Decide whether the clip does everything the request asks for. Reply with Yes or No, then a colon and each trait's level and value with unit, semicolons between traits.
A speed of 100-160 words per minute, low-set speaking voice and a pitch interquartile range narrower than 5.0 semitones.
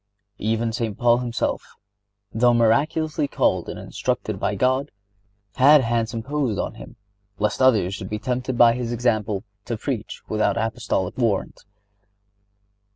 Yes: average, 140 wpm; low, 115 Hz; average, 2.7 semitones